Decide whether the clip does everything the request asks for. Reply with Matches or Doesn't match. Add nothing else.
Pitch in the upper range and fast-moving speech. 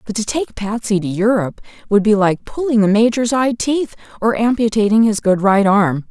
Doesn't match